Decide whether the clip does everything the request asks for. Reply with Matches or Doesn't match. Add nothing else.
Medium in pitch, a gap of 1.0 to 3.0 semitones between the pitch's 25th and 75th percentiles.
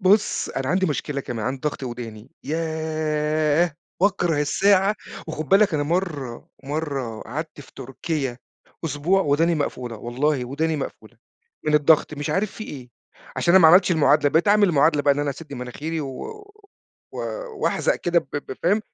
Doesn't match